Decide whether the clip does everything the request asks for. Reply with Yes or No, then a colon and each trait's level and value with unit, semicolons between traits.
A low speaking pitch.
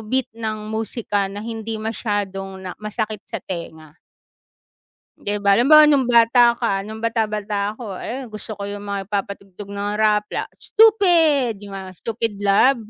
No: high, 215 Hz